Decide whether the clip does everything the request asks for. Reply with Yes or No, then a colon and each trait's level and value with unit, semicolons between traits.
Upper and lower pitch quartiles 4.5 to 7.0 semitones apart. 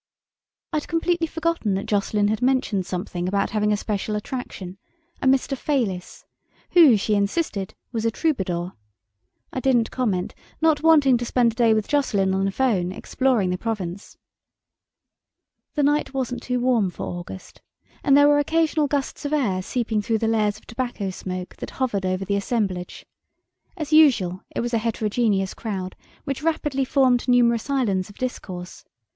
Yes: wide, 5.5 semitones